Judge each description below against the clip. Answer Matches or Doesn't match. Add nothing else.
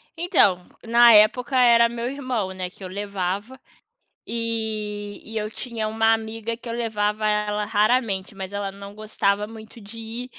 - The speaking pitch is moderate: Doesn't match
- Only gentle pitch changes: Matches